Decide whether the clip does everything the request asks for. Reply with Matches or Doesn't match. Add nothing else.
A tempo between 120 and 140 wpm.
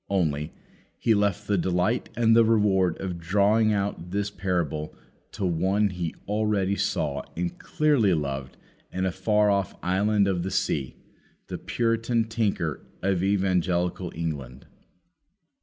Matches